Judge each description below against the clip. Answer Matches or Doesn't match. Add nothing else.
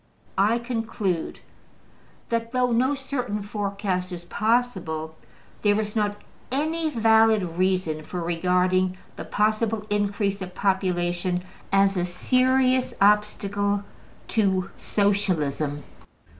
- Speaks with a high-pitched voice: Matches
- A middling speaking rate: Doesn't match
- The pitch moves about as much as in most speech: Matches